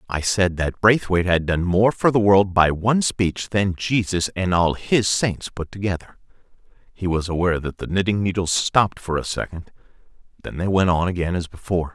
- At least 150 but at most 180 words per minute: No, average, 195 wpm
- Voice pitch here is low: Yes, very low, 95 Hz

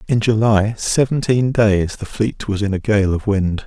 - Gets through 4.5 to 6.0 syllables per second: No, 4.3 syllables/s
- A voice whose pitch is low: Yes, low, 105 Hz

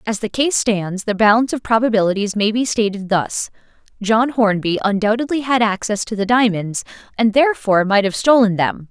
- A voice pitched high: Yes, high, 215 Hz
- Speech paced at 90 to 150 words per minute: No, average, 175 wpm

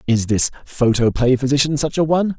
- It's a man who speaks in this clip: Yes, male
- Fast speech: No, average, 175 wpm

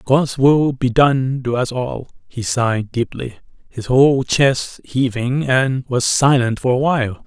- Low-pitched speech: Yes, low, 130 Hz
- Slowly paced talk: No, average, 165 wpm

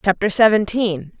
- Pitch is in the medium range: No, high, 200 Hz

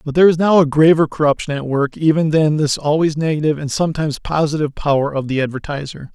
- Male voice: Yes, male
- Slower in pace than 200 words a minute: No, fast, 205 wpm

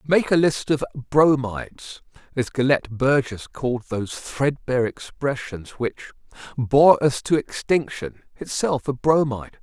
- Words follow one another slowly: Yes, slow, 120 wpm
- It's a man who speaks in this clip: Yes, male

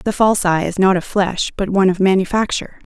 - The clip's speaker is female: Yes, female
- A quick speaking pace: Yes, fast, 225 wpm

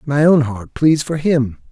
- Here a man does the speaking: Yes, male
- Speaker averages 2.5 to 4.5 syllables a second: Yes, 4.0 syllables/s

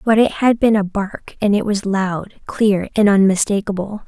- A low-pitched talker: No, high, 205 Hz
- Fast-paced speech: No, average, 190 wpm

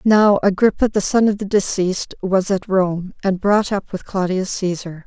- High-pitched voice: Yes, high, 195 Hz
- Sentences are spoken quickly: No, average, 190 wpm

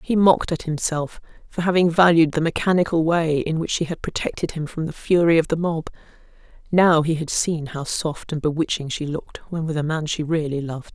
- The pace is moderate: No, fast, 215 wpm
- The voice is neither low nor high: Yes, medium, 160 Hz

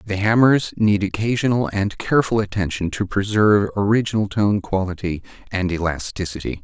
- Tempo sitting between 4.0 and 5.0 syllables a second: No, 5.4 syllables/s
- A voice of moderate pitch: No, low, 100 Hz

